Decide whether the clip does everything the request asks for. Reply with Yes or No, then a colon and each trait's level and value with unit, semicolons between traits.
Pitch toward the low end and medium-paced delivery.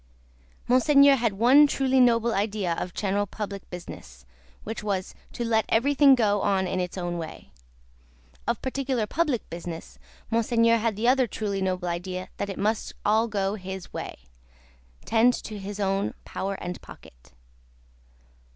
No: high, 210 Hz; average, 150 wpm